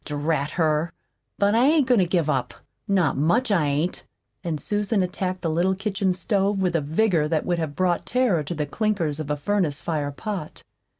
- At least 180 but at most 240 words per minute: Yes, average, 195 wpm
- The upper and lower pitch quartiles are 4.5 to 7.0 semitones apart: Yes, average, 4.8 semitones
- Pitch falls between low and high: Yes, medium, 175 Hz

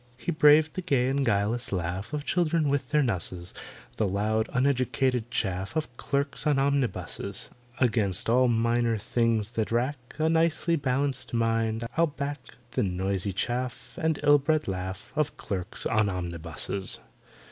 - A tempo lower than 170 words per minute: Yes, average, 145 wpm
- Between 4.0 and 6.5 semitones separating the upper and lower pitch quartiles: Yes, average, 5.3 semitones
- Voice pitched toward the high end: No, low, 120 Hz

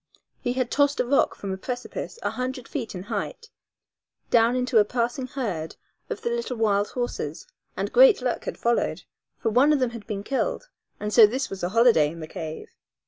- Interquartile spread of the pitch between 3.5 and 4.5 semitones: Yes, average, 4.0 semitones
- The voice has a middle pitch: No, high, 240 Hz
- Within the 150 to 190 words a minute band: No, average, 200 wpm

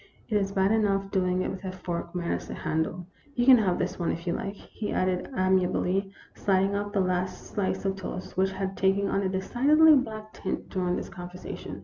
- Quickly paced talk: Yes, fast, 215 wpm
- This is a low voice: No, high, 190 Hz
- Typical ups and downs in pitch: No, narrow, 1.7 semitones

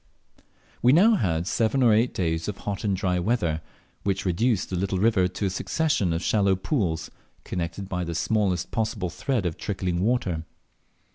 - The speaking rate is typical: Yes, average, 170 wpm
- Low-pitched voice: Yes, very low, 95 Hz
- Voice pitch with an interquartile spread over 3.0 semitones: Yes, average, 3.9 semitones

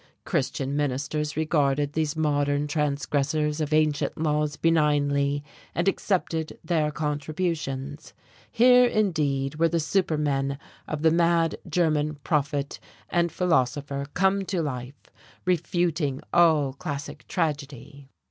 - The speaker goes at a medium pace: No, slow, 110 wpm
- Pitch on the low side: No, medium, 150 Hz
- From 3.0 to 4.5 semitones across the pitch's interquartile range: No, narrow, 2.5 semitones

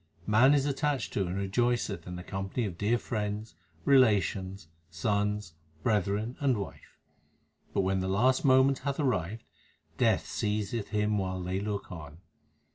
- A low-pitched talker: Yes, low, 105 Hz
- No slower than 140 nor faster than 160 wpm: Yes, average, 145 wpm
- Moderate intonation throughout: Yes, average, 4.0 semitones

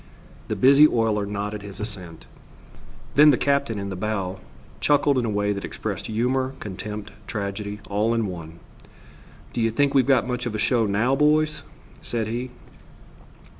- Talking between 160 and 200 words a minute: Yes, average, 165 wpm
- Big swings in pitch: No, average, 4.2 semitones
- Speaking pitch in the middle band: No, low, 110 Hz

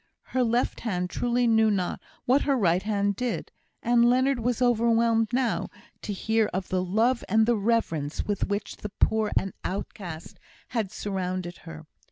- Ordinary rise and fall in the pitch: Yes, average, 4.0 semitones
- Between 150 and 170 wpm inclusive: Yes, average, 165 wpm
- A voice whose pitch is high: Yes, high, 220 Hz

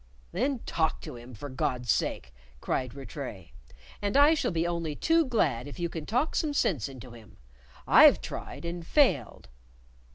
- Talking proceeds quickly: No, average, 165 wpm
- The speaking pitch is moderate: Yes, medium, 160 Hz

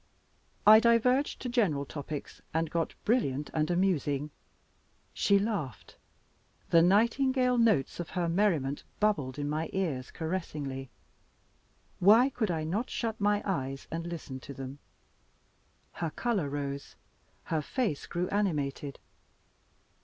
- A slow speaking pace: Yes, slow, 125 wpm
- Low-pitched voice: No, medium, 170 Hz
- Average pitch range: No, wide, 6.7 semitones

